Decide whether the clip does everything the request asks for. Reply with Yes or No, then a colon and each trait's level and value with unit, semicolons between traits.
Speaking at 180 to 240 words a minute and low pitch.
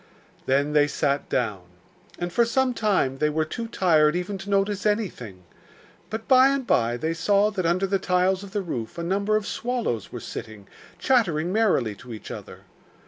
No: average, 185 wpm; medium, 185 Hz